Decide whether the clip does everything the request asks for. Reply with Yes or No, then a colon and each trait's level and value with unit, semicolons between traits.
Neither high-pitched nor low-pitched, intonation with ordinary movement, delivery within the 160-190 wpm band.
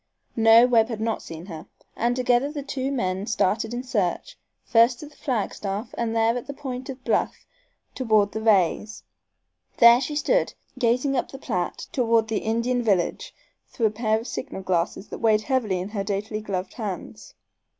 No: high, 225 Hz; average, 3.2 semitones; average, 175 wpm